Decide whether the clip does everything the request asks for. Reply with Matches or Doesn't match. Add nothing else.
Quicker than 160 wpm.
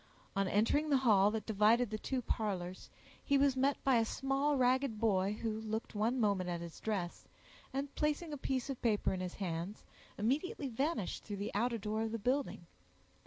Matches